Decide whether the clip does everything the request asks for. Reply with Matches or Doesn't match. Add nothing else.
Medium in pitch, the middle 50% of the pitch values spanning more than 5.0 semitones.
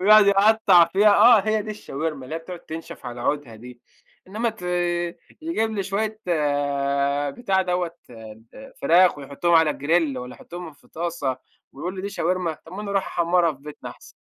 Matches